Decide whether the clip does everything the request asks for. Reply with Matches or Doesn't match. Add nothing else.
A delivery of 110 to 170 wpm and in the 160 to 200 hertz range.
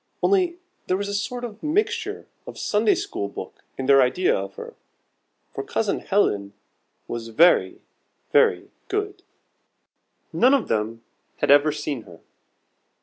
Matches